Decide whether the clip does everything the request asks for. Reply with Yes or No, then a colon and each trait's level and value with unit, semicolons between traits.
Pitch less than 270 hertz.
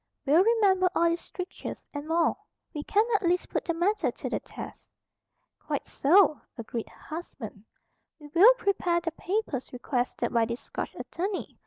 No: very high, 340 Hz